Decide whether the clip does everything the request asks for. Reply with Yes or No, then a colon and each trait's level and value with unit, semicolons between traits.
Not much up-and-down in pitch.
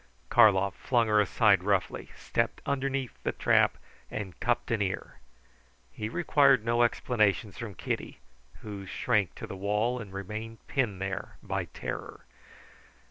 No: average, 3.3 semitones